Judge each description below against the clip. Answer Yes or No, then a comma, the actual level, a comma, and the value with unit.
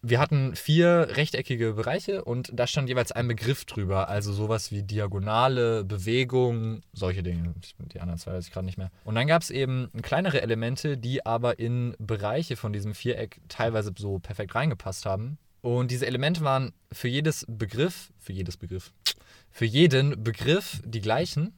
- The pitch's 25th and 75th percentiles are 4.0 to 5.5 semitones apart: Yes, average, 4.3 semitones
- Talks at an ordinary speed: Yes, average, 170 wpm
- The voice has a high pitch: No, low, 120 Hz